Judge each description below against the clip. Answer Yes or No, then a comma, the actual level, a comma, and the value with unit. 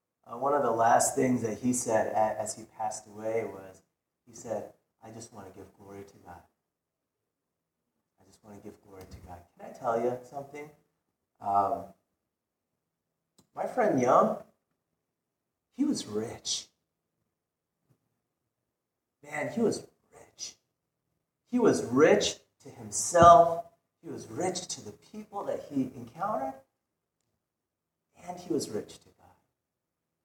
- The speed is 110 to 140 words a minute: Yes, slow, 135 wpm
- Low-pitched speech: Yes, low, 110 Hz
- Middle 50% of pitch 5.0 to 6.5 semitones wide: Yes, wide, 5.6 semitones